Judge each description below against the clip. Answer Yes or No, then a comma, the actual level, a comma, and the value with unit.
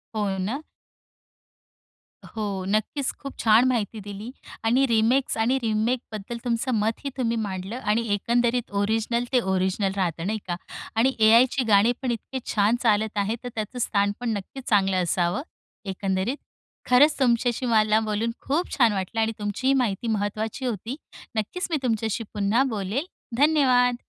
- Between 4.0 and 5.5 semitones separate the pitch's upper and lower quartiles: No, average, 3.2 semitones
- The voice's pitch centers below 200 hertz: No, high, 225 Hz